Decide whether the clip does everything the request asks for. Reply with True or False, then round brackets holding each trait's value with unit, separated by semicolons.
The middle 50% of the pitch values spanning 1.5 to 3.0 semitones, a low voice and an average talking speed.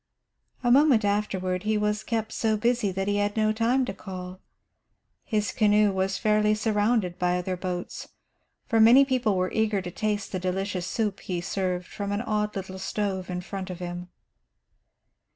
False (2.7 semitones; 205 Hz; 170 wpm)